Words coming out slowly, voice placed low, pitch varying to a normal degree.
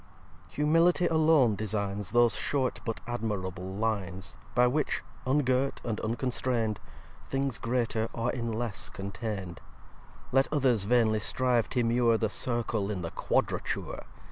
Yes: slow, 125 wpm; low, 115 Hz; average, 3.3 semitones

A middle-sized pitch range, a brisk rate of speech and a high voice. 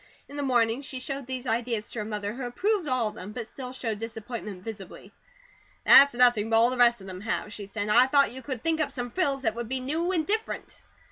Yes: average, 3.5 semitones; fast, 245 wpm; high, 245 Hz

